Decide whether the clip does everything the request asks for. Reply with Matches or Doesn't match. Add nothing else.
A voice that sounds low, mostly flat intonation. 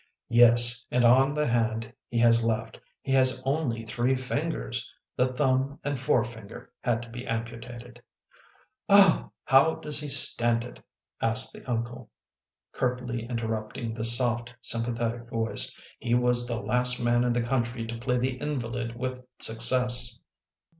Matches